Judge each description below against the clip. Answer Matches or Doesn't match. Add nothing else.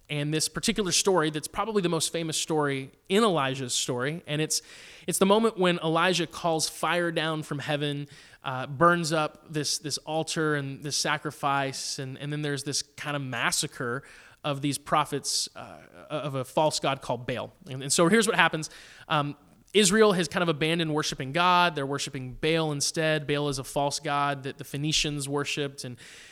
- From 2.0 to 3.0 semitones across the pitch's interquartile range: Matches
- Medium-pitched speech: Matches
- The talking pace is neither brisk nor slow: Matches